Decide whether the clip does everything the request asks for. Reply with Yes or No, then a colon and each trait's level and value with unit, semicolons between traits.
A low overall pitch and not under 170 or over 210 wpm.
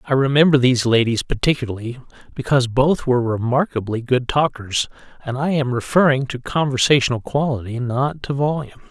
No: low, 130 Hz; slow, 135 wpm